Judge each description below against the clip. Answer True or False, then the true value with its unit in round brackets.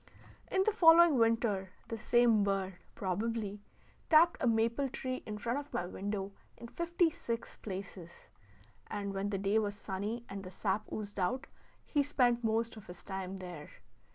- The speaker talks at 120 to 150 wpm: False (165 wpm)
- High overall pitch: True (215 Hz)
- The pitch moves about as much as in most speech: True (3.8 semitones)